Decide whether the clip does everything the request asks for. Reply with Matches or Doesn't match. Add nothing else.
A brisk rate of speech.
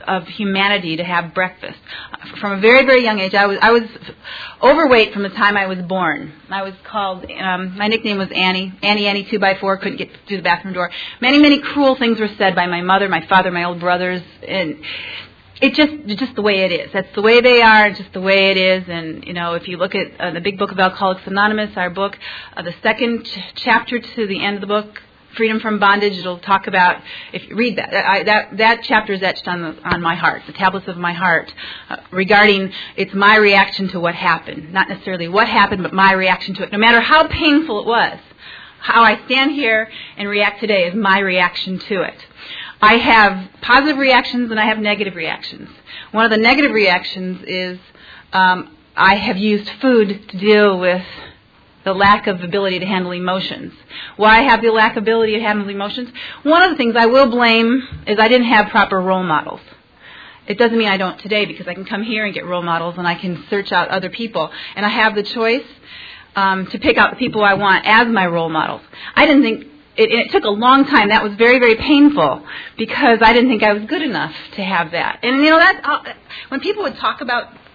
Matches